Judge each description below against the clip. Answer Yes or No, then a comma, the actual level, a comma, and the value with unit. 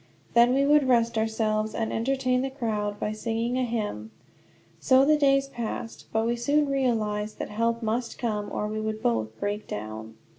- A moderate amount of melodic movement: Yes, average, 3.2 semitones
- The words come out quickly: No, average, 180 wpm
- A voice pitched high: Yes, high, 230 Hz